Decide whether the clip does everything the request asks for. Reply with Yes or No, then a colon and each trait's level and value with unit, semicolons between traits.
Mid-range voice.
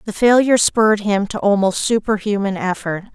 No: high, 205 Hz